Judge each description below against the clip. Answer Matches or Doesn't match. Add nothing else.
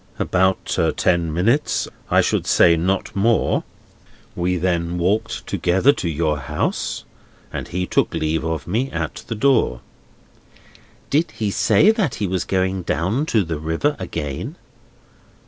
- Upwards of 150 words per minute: Doesn't match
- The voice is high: Doesn't match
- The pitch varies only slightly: Doesn't match